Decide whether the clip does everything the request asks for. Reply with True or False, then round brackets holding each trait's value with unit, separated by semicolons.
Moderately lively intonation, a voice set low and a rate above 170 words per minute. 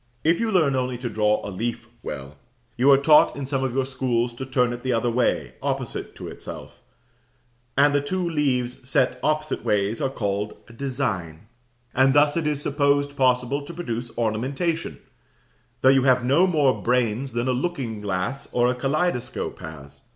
True (3.1 semitones; 130 Hz; 180 wpm)